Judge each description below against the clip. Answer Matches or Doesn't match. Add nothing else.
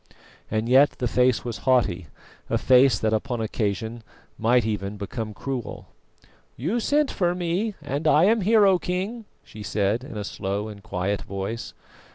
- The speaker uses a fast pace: Doesn't match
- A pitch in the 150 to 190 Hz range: Doesn't match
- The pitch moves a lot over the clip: Matches